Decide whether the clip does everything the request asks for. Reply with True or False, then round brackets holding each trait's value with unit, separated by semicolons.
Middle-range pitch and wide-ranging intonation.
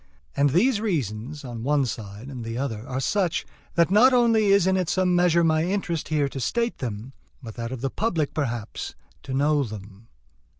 True (145 Hz; 7.3 semitones)